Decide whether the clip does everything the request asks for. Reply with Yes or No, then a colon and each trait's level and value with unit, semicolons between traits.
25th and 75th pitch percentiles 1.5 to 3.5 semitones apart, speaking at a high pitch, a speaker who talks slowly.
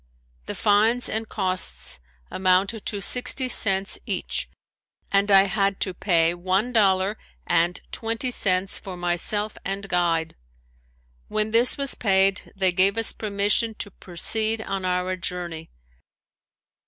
Yes: average, 2.8 semitones; high, 195 Hz; slow, 130 wpm